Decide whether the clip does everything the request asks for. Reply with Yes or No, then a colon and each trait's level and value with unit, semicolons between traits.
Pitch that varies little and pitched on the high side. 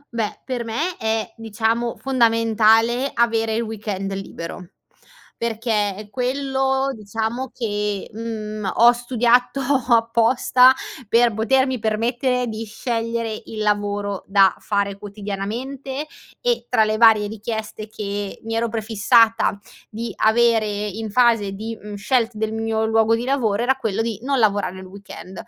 Yes: narrow, 2.1 semitones; high, 225 Hz